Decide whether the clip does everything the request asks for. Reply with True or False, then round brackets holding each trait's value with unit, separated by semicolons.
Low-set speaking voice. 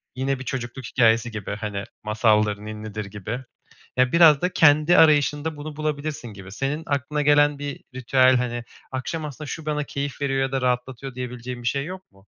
True (130 Hz)